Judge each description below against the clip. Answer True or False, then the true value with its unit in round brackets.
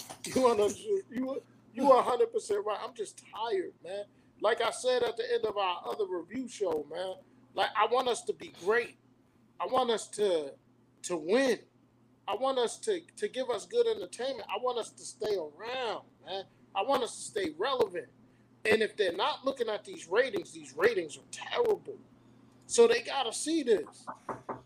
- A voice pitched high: True (360 Hz)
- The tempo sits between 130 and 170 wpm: False (185 wpm)